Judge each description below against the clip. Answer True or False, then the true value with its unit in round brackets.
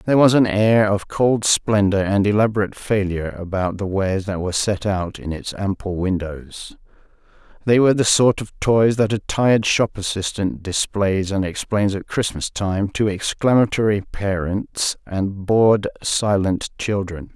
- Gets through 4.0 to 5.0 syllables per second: True (4.6 syllables/s)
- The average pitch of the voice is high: False (100 Hz)